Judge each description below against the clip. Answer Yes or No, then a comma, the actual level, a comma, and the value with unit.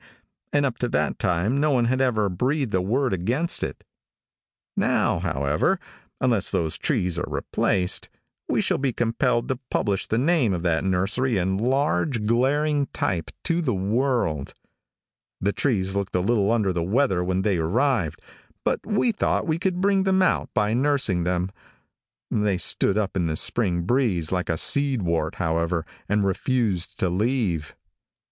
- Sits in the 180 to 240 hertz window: No, low, 105 Hz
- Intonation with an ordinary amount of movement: No, wide, 6.6 semitones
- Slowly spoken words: No, average, 165 wpm